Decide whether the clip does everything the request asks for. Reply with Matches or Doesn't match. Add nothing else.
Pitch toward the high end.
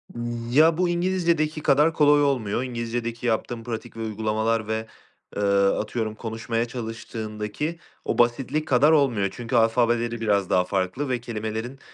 Doesn't match